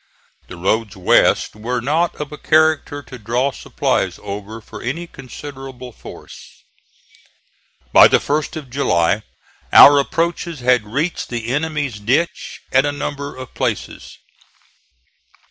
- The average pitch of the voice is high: No, low, 135 Hz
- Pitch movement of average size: Yes, average, 4.2 semitones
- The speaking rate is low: Yes, slow, 130 wpm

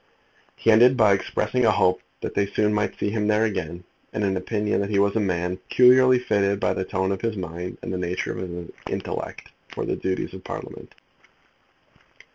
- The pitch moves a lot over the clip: No, average, 2.7 semitones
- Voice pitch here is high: No, low, 100 Hz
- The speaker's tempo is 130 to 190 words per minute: No, average, 200 wpm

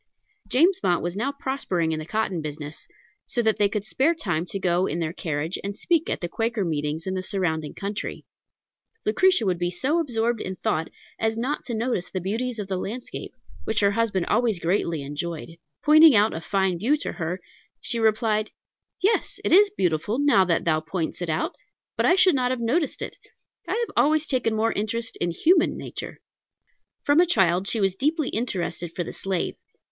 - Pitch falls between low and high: No, high, 205 Hz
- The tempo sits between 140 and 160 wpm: No, average, 195 wpm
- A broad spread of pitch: Yes, wide, 6.4 semitones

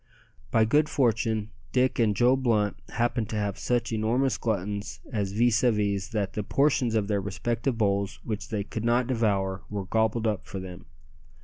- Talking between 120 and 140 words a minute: No, average, 180 wpm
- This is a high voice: No, low, 110 Hz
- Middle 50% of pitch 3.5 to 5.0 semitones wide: No, average, 2.7 semitones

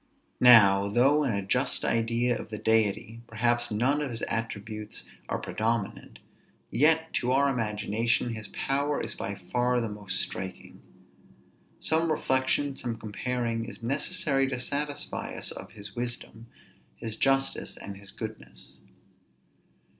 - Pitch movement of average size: Yes, average, 3.8 semitones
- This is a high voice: No, low, 115 Hz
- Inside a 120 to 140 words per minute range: Yes, slow, 135 wpm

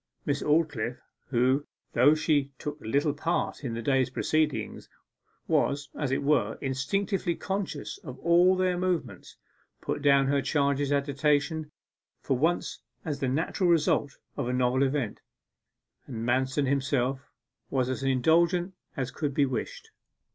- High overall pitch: No, medium, 140 Hz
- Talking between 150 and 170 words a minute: No, average, 140 wpm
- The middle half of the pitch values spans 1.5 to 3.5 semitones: Yes, average, 3.2 semitones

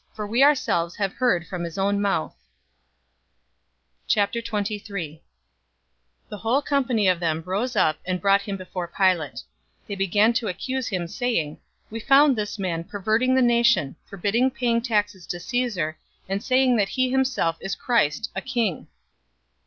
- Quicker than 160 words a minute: No, average, 155 wpm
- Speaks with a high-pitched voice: Yes, high, 205 Hz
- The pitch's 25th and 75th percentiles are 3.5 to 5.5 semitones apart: Yes, average, 4.9 semitones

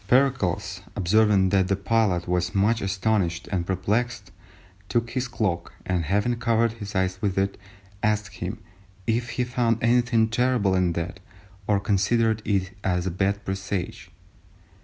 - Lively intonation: No, average, 3.6 semitones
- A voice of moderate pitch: No, low, 100 Hz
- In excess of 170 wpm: No, average, 145 wpm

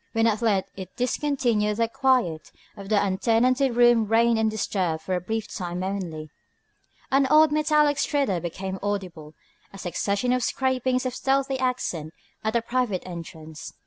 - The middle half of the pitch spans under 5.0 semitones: No, average, 5.3 semitones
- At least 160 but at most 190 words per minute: No, average, 150 wpm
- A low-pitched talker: No, high, 220 Hz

